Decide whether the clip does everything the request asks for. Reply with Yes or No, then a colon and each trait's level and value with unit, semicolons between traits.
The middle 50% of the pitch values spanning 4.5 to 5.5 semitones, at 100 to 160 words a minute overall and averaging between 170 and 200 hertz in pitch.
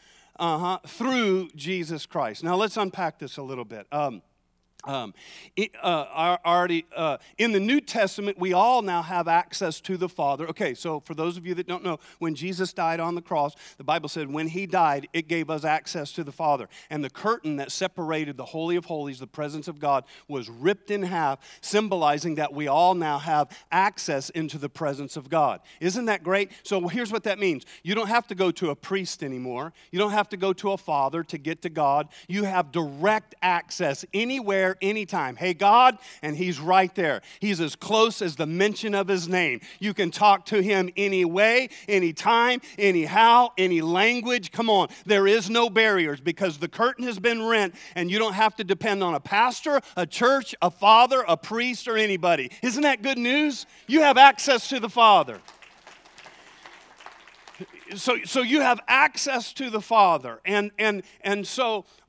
No: average, 5.0 semitones; average, 190 wpm; medium, 185 Hz